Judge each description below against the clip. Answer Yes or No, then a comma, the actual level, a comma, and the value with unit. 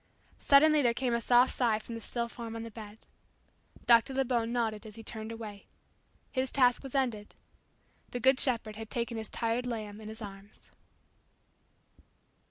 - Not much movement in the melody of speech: Yes, narrow, 2.2 semitones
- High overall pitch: Yes, high, 230 Hz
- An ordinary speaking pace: Yes, average, 170 wpm